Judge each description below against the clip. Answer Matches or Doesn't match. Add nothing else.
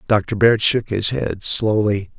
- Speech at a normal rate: Matches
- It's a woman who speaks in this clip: Doesn't match